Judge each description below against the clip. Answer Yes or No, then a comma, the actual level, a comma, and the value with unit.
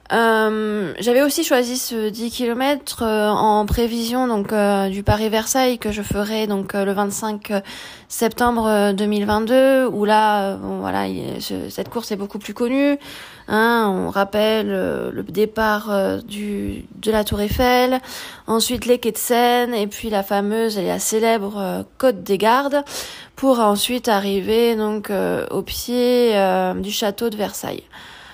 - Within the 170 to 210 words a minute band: No, average, 160 wpm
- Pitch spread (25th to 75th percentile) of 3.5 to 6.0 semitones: No, average, 2.9 semitones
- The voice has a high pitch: Yes, high, 215 Hz